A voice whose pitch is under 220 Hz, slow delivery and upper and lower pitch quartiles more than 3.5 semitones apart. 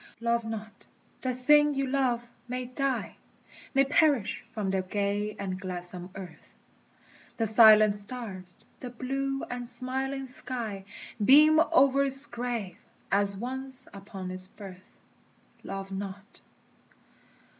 No: high, 235 Hz; slow, 120 wpm; average, 5.0 semitones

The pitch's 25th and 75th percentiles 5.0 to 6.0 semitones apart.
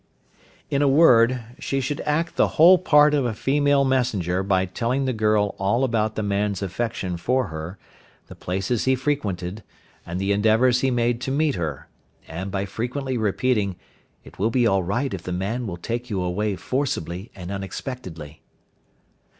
Yes: wide, 5.4 semitones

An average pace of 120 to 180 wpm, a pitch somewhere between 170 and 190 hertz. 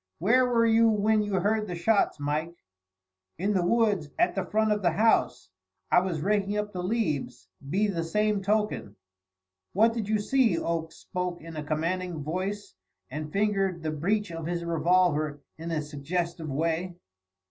Yes: average, 170 wpm; medium, 185 Hz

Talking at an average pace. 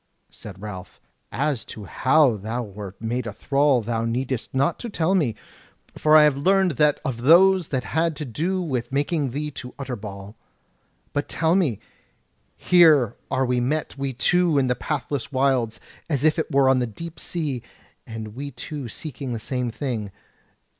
Yes: average, 170 wpm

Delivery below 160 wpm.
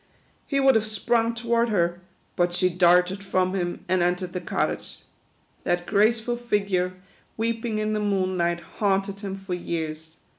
Yes: average, 150 wpm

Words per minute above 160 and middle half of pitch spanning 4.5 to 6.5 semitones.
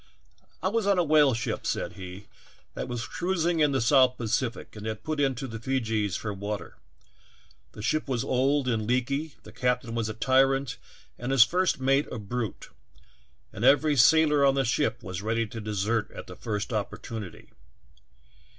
No: average, 175 wpm; average, 4.0 semitones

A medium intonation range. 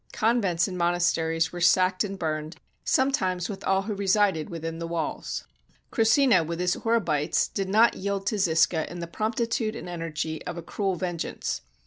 Yes: average, 3.6 semitones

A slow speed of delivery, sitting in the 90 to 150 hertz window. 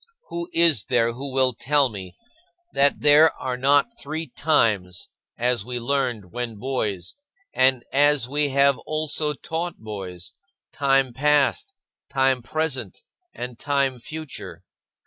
Yes: slow, 125 wpm; low, 135 Hz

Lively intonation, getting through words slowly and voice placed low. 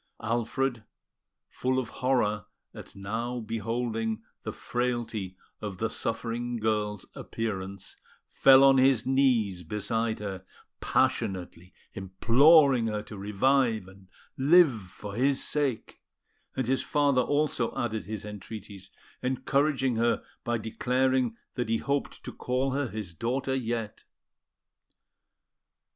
No: average, 3.7 semitones; slow, 115 wpm; low, 115 Hz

